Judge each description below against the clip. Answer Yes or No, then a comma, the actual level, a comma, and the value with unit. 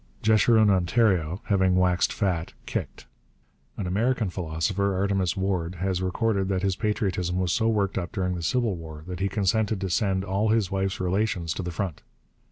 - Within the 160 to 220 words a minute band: Yes, average, 175 wpm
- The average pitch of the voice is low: Yes, very low, 95 Hz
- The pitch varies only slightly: Yes, narrow, 2.3 semitones